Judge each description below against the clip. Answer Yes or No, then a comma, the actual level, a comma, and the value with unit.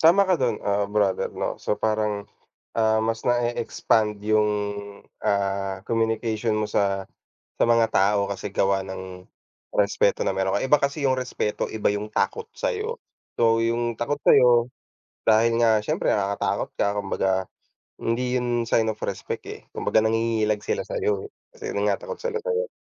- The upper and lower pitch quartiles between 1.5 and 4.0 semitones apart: Yes, average, 3.6 semitones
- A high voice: No, low, 115 Hz